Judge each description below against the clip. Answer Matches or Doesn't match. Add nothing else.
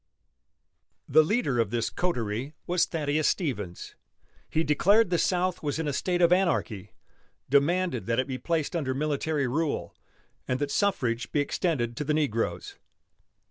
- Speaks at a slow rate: Doesn't match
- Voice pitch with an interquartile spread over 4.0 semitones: Matches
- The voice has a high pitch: Doesn't match